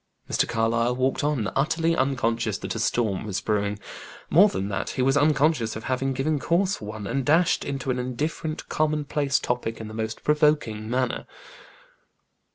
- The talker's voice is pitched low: Yes, low, 130 Hz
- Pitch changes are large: No, average, 4.9 semitones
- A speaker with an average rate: Yes, average, 170 wpm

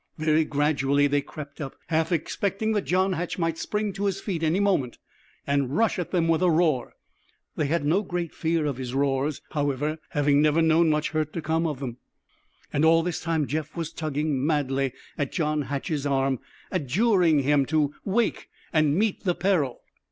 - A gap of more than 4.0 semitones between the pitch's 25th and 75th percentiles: No, average, 3.3 semitones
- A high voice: No, medium, 155 Hz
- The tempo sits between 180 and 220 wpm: Yes, average, 185 wpm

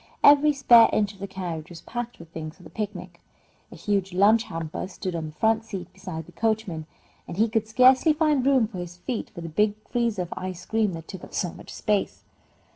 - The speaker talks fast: Yes, fast, 220 wpm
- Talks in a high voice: Yes, high, 195 Hz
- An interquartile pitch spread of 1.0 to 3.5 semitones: No, average, 4.5 semitones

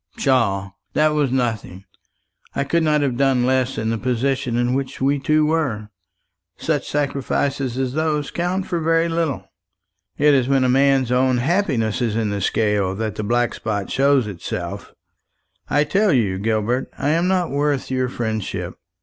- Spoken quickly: No, average, 165 wpm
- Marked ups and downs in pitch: No, average, 4.3 semitones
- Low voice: Yes, low, 130 Hz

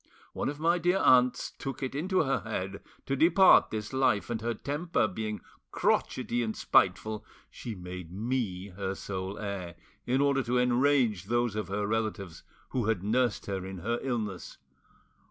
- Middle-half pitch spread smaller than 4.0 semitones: No, average, 4.9 semitones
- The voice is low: Yes, low, 110 Hz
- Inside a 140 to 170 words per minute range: Yes, average, 165 wpm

